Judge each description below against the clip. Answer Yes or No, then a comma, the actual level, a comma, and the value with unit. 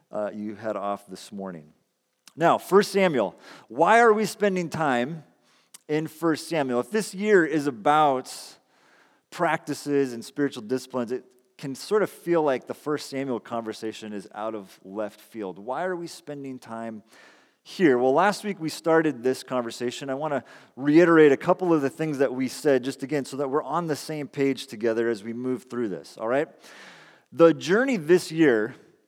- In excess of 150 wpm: Yes, average, 180 wpm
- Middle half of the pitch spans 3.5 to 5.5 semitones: Yes, average, 5.2 semitones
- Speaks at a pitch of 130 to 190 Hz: Yes, medium, 140 Hz